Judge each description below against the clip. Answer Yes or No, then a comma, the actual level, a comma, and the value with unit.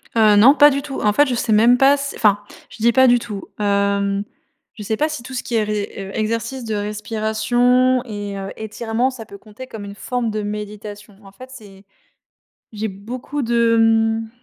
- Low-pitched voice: No, high, 220 Hz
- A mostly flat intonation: No, average, 3.1 semitones